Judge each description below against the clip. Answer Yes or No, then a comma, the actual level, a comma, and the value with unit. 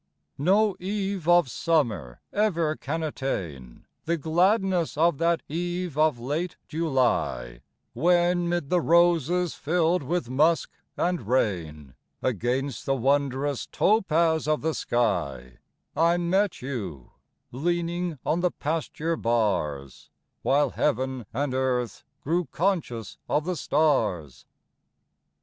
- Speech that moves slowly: Yes, slow, 115 wpm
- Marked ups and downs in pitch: Yes, wide, 5.9 semitones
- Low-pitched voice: No, medium, 155 Hz